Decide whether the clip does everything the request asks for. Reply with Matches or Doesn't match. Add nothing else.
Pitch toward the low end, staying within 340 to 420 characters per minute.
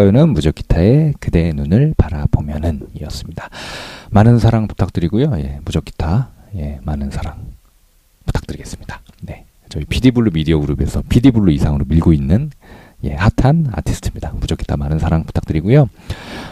Matches